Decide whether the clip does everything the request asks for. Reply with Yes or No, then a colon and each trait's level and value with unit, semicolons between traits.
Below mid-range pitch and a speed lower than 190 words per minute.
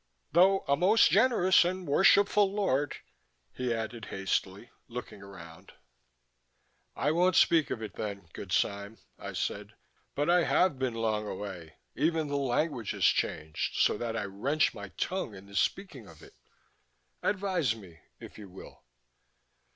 Yes: low, 125 Hz; average, 150 wpm